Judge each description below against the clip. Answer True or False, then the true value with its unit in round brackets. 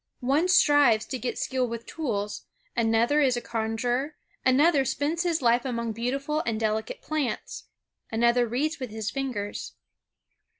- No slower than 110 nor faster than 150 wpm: True (140 wpm)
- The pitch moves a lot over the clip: False (4.3 semitones)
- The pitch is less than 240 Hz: False (245 Hz)